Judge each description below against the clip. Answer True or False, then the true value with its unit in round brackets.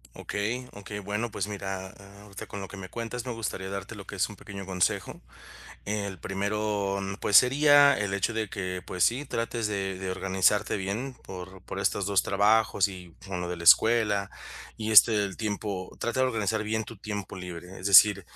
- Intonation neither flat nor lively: False (2.3 semitones)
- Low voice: True (100 Hz)